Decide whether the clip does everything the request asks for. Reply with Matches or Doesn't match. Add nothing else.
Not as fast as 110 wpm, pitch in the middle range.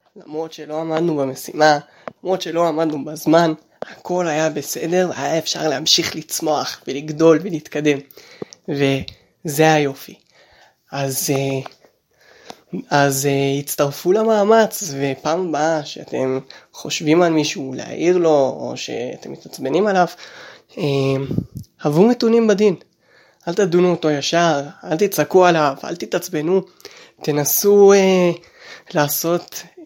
Matches